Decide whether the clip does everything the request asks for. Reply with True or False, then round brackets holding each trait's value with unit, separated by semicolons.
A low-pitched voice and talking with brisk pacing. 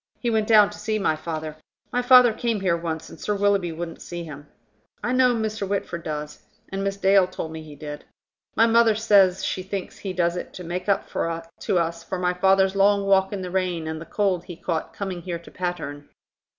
False (185 Hz; 215 wpm)